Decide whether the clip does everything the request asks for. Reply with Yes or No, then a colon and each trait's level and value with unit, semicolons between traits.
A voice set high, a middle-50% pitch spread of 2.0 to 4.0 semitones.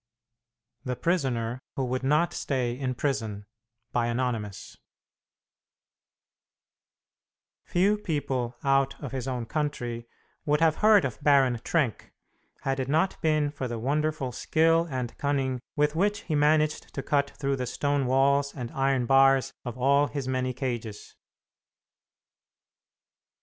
No: low, 135 Hz; average, 3.0 semitones